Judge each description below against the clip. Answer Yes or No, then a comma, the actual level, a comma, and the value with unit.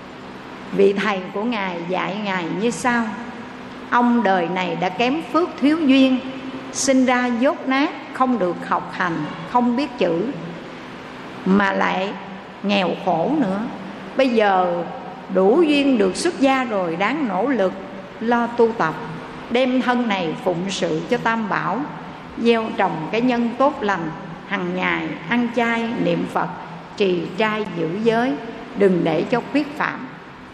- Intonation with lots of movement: No, average, 5.0 semitones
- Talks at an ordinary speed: No, slow, 145 wpm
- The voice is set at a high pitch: Yes, high, 225 Hz